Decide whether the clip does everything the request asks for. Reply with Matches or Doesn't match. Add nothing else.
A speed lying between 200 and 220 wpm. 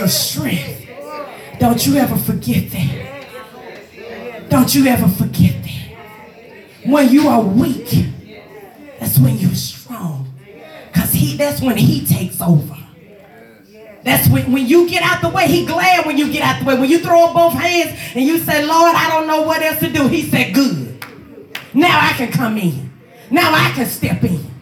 Doesn't match